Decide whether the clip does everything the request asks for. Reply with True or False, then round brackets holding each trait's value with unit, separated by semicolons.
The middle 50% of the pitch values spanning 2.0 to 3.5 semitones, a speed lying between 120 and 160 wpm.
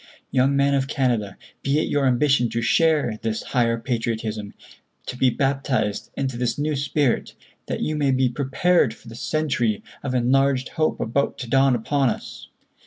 False (3.1 semitones; 170 wpm)